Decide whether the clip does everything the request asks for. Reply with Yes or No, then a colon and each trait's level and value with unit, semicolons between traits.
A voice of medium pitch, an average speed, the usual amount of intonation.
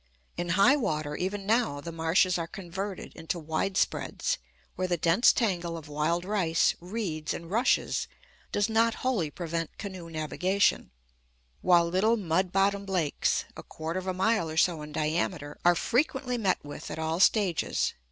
Yes: medium, 180 Hz; average, 160 wpm; average, 3.6 semitones